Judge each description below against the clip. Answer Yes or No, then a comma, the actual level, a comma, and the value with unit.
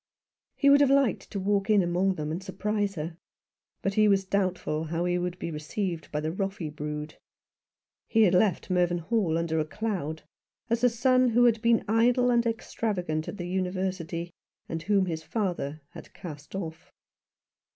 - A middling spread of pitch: Yes, average, 4.8 semitones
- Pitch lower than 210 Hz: Yes, medium, 185 Hz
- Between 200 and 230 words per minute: No, average, 170 wpm